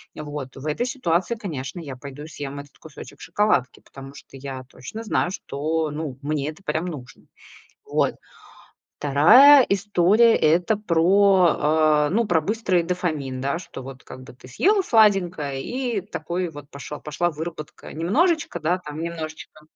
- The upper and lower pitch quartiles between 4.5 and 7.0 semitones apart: Yes, average, 5.2 semitones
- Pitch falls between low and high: Yes, medium, 160 Hz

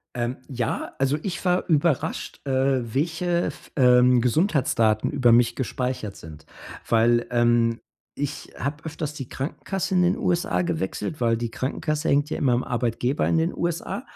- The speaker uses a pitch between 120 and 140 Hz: Yes, low, 135 Hz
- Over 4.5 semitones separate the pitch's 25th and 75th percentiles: Yes, average, 5.3 semitones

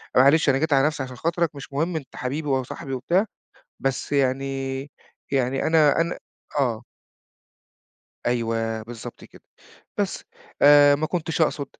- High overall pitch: No, medium, 140 Hz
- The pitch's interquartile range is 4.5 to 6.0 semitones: No, average, 3.4 semitones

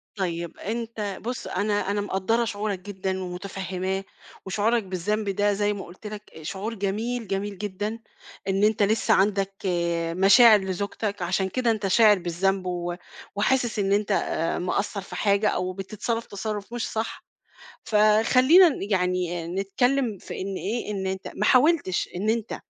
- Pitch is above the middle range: Yes, high, 205 Hz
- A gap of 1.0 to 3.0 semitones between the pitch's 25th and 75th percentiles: Yes, narrow, 2.5 semitones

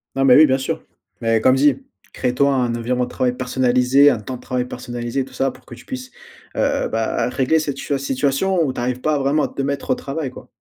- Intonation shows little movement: Yes, narrow, 2.1 semitones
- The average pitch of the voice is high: No, low, 130 Hz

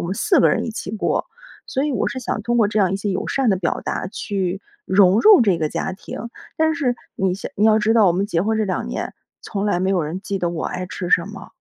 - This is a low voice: No, high, 200 Hz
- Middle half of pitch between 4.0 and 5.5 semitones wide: No, average, 3.2 semitones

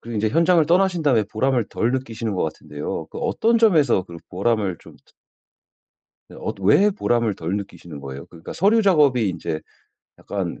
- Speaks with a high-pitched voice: No, low, 115 Hz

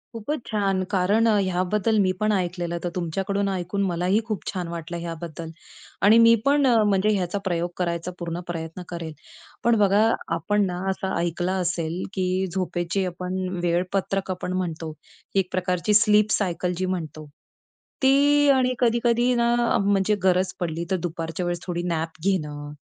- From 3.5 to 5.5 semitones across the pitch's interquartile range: No, average, 2.9 semitones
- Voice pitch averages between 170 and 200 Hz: Yes, medium, 185 Hz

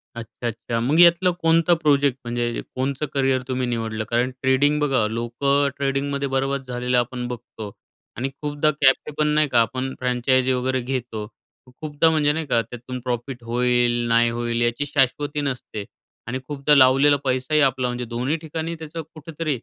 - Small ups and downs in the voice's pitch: No, average, 3.1 semitones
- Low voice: Yes, low, 130 Hz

